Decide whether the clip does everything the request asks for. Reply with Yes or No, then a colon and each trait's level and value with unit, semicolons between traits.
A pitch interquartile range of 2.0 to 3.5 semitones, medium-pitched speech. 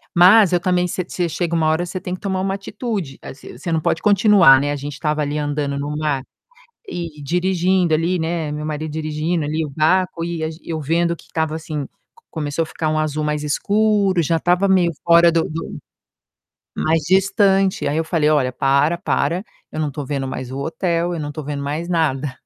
Yes: average, 3.1 semitones; medium, 160 Hz